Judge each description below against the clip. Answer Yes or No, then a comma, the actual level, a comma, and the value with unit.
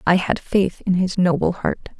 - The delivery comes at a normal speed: No, fast, 210 wpm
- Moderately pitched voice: Yes, medium, 180 Hz